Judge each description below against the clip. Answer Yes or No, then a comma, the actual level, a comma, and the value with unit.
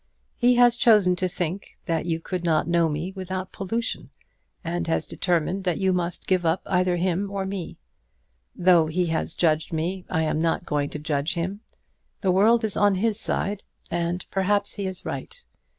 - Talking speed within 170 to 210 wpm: Yes, average, 180 wpm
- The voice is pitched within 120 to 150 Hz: No, medium, 180 Hz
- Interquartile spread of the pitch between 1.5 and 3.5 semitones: Yes, average, 2.8 semitones